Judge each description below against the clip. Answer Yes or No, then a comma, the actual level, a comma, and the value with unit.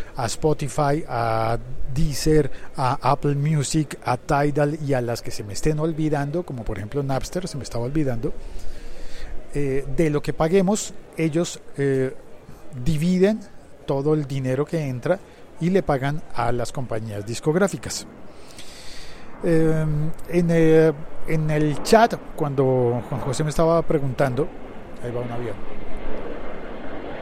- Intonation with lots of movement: No, average, 3.8 semitones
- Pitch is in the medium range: Yes, medium, 145 Hz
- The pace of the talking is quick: No, average, 135 wpm